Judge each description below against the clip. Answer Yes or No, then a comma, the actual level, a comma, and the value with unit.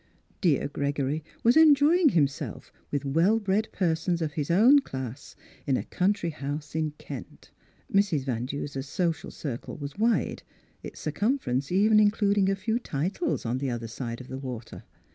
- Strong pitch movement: Yes, wide, 7.0 semitones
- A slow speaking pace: No, average, 165 wpm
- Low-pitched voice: No, medium, 160 Hz